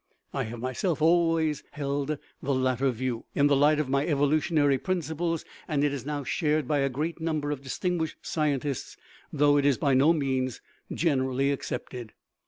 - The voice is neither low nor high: Yes, medium, 145 Hz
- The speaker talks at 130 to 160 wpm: No, average, 170 wpm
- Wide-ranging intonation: No, narrow, 2.6 semitones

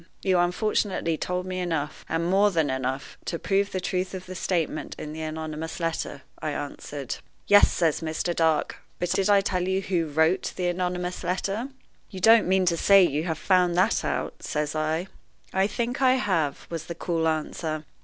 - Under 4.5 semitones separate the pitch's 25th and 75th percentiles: Yes, average, 3.0 semitones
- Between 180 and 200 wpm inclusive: Yes, average, 190 wpm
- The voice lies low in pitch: No, medium, 175 Hz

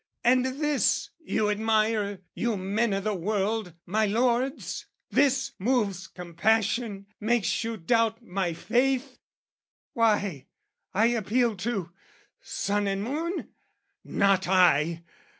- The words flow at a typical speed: No, slow, 105 wpm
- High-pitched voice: Yes, high, 215 Hz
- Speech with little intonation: No, average, 3.6 semitones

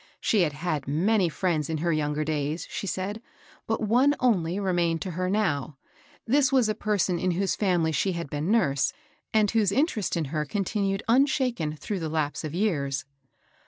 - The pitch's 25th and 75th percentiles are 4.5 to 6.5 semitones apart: Yes, wide, 5.5 semitones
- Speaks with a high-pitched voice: No, medium, 180 Hz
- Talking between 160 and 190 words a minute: Yes, average, 185 wpm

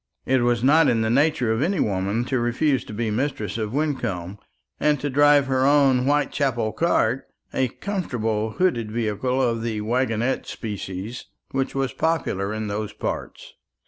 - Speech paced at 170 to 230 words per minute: No, average, 160 wpm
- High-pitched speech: No, low, 120 Hz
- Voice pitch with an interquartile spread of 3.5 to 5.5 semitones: Yes, average, 4.2 semitones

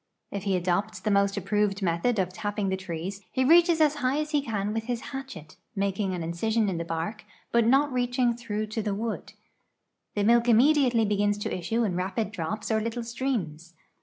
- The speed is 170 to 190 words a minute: No, average, 200 wpm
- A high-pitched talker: Yes, high, 215 Hz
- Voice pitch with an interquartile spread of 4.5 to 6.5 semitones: No, average, 4.0 semitones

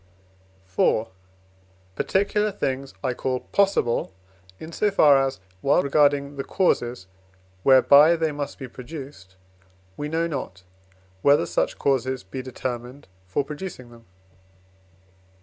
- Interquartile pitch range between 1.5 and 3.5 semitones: Yes, average, 3.2 semitones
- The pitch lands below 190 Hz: Yes, low, 135 Hz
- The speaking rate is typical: No, slow, 115 wpm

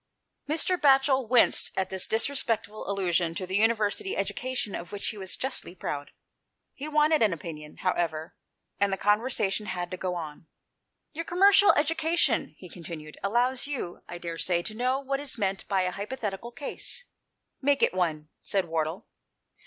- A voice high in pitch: Yes, high, 205 Hz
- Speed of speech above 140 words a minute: Yes, average, 170 wpm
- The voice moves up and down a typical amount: No, wide, 7.1 semitones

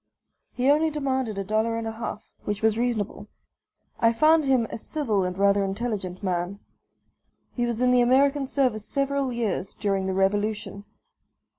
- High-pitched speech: Yes, high, 225 Hz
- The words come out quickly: No, average, 160 wpm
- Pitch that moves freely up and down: No, average, 4.5 semitones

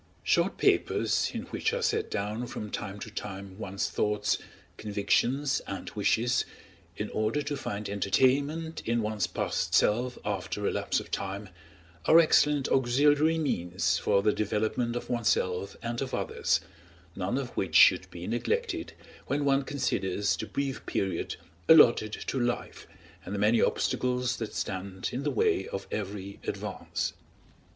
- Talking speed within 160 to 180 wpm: No, average, 150 wpm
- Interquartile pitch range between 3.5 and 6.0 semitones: Yes, average, 5.2 semitones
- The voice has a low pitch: Yes, low, 110 Hz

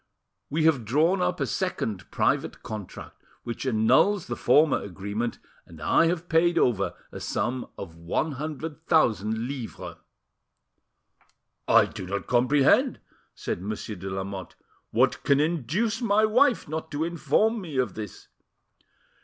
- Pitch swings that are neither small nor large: No, wide, 7.6 semitones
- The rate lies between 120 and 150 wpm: Yes, slow, 135 wpm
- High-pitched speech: No, low, 135 Hz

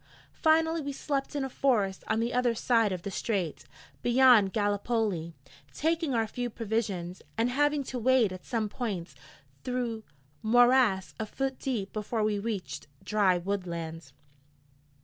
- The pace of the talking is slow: No, average, 145 wpm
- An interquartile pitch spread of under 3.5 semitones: No, average, 4.2 semitones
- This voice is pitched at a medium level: No, high, 225 Hz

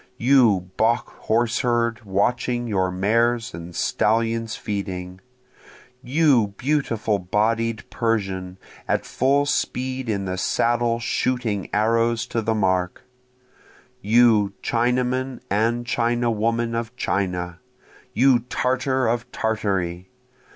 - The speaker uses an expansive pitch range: No, average, 3.3 semitones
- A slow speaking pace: Yes, slow, 100 wpm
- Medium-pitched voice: No, low, 115 Hz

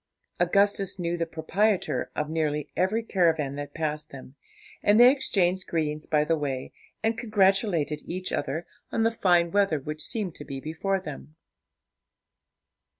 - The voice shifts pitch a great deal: No, average, 4.6 semitones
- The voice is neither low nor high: Yes, medium, 170 Hz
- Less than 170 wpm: Yes, average, 150 wpm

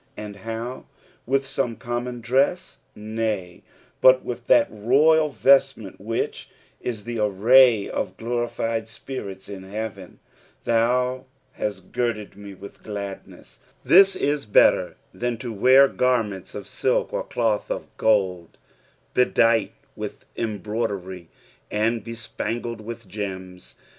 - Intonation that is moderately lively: Yes, average, 3.3 semitones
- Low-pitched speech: Yes, low, 115 Hz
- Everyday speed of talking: No, slow, 120 wpm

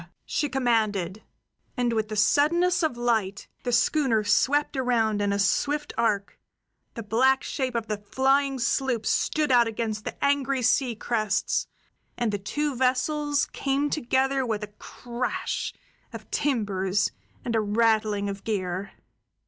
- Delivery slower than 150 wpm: Yes, average, 140 wpm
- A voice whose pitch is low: No, high, 235 Hz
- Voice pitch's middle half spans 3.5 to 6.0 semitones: Yes, average, 4.1 semitones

